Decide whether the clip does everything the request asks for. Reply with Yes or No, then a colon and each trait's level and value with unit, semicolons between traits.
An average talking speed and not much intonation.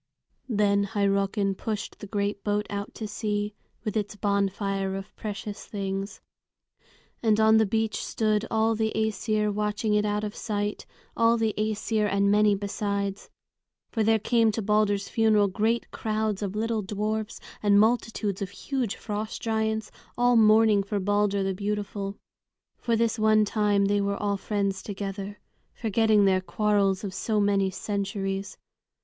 Yes: average, 150 wpm; narrow, 1.5 semitones